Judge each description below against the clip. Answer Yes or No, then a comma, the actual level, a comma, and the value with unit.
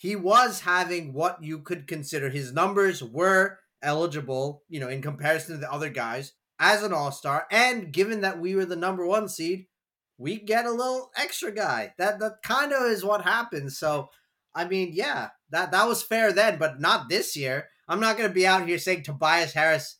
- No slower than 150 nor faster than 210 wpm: Yes, average, 200 wpm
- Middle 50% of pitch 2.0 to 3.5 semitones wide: No, average, 5.0 semitones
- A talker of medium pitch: Yes, medium, 180 Hz